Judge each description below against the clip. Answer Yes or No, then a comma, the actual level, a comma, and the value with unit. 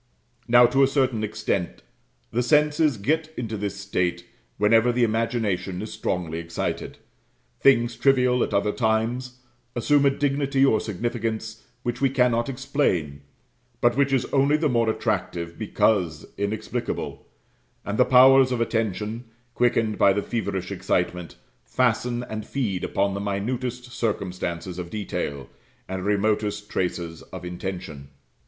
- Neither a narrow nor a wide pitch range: Yes, average, 4.5 semitones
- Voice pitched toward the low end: Yes, low, 110 Hz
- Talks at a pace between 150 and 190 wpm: No, slow, 135 wpm